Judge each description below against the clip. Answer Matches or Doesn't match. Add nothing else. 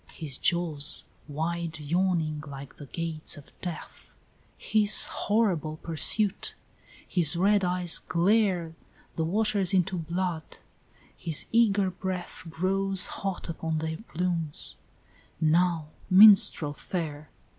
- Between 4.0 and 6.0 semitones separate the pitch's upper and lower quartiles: Doesn't match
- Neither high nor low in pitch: Matches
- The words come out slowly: Matches